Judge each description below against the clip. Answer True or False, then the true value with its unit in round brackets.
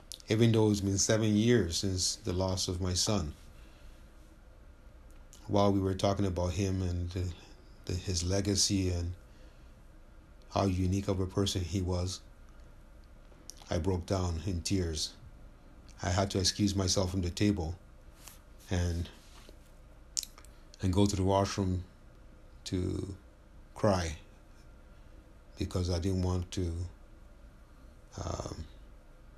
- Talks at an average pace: False (120 wpm)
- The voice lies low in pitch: True (95 Hz)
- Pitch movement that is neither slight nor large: True (3.0 semitones)